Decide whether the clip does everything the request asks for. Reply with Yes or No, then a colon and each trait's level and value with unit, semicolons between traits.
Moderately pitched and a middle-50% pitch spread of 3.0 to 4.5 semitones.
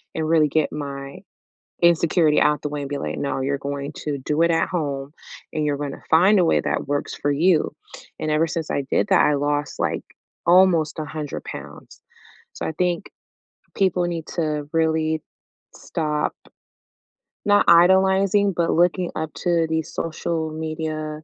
No: medium, 155 Hz; narrow, 2.5 semitones